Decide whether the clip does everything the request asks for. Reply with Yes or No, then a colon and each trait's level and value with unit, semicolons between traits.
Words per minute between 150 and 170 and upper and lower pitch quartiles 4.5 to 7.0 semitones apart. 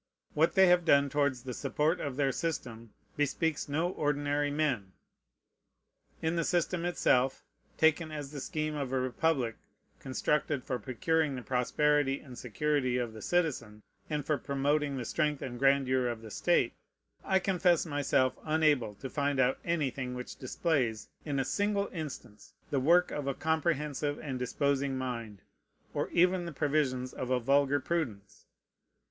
No: average, 155 wpm; average, 3.5 semitones